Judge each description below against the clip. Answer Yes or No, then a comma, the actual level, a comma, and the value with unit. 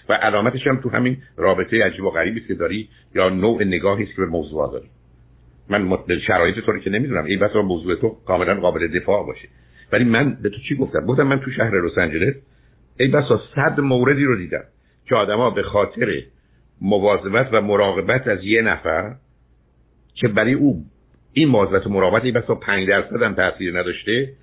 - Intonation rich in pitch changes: Yes, wide, 7.2 semitones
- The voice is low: Yes, low, 105 Hz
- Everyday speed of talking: No, fast, 180 wpm